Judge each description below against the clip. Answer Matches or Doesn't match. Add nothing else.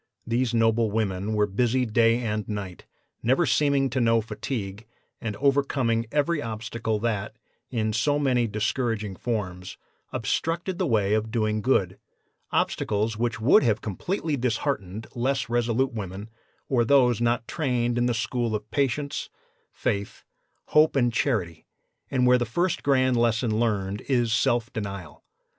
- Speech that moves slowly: Doesn't match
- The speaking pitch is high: Doesn't match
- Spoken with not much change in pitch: Doesn't match